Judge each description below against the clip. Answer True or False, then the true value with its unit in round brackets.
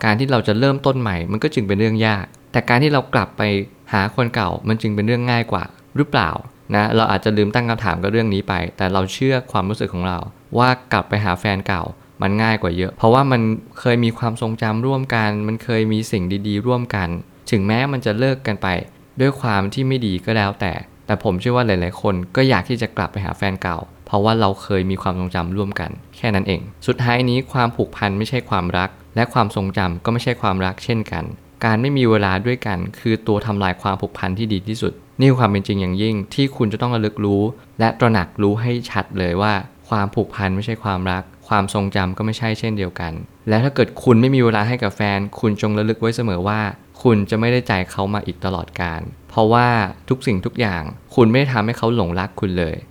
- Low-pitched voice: True (105 Hz)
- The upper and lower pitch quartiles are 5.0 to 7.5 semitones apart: False (3.6 semitones)